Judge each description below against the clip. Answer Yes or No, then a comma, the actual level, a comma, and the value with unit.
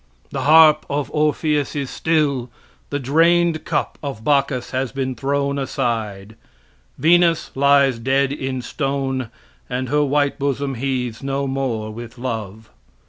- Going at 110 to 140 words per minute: Yes, slow, 135 wpm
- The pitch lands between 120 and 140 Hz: Yes, low, 135 Hz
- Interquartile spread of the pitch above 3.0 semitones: No, narrow, 2.4 semitones